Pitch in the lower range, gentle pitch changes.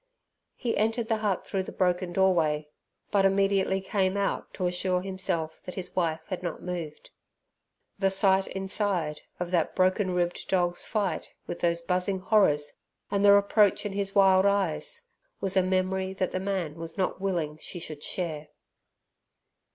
No: medium, 185 Hz; narrow, 2.1 semitones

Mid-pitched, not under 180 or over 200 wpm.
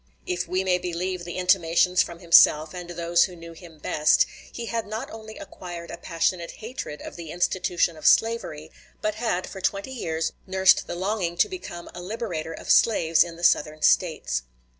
Yes: medium, 175 Hz; average, 185 wpm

